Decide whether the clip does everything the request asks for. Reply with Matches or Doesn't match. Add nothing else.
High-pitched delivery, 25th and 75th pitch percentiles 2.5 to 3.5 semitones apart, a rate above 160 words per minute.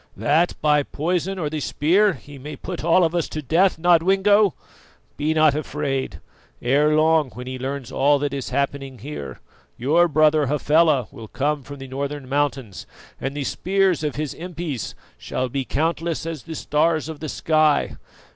Doesn't match